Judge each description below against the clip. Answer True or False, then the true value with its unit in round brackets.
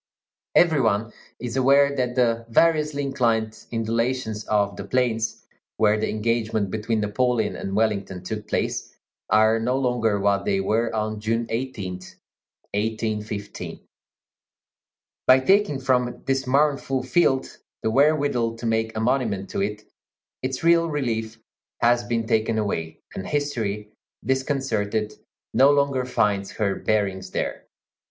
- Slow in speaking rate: True (130 wpm)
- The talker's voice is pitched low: True (115 Hz)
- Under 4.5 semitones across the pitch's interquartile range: True (3.6 semitones)